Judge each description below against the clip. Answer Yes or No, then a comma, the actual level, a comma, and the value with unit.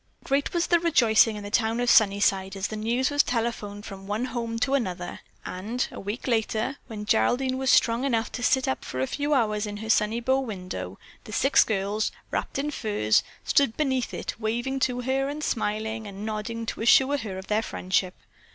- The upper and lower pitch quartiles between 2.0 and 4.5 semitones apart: Yes, average, 3.9 semitones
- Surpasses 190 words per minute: Yes, average, 200 wpm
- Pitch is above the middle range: Yes, high, 225 Hz